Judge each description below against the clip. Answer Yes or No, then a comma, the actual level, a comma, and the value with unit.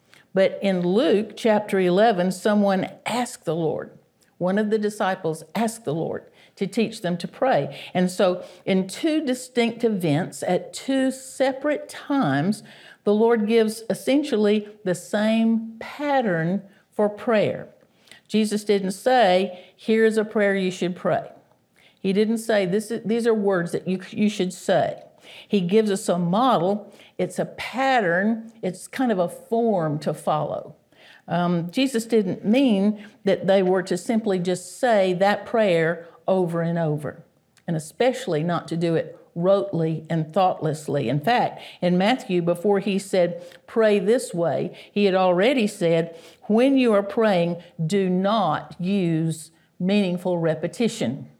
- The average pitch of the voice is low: No, high, 195 Hz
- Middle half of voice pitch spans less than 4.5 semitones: Yes, average, 4.0 semitones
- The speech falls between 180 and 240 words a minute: No, average, 145 wpm